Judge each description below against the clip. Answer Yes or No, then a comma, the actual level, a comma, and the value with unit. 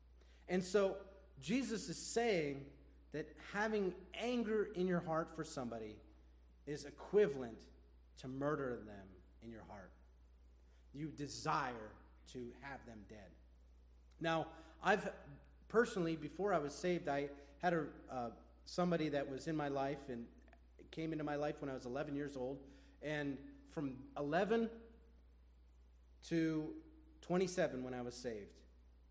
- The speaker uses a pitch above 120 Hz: Yes, medium, 140 Hz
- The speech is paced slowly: Yes, slow, 130 wpm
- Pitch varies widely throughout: Yes, wide, 8.0 semitones